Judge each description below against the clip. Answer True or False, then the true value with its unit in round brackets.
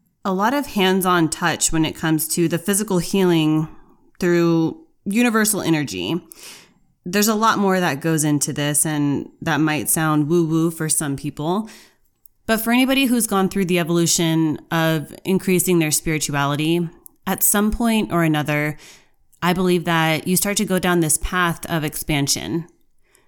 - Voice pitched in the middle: True (170 Hz)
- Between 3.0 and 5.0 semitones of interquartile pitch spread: True (3.4 semitones)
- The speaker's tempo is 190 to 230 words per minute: False (160 wpm)